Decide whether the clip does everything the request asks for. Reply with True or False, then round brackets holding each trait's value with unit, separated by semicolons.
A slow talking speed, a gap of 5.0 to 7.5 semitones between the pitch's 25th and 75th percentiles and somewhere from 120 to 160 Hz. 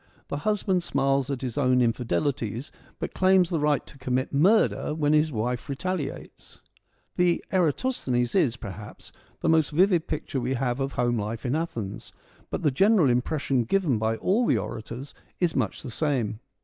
False (165 wpm; 5.3 semitones; 140 Hz)